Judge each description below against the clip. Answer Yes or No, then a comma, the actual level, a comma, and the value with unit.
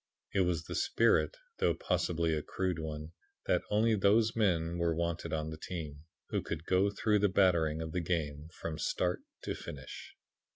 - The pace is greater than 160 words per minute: Yes, average, 175 wpm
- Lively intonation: No, average, 3.0 semitones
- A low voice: Yes, very low, 85 Hz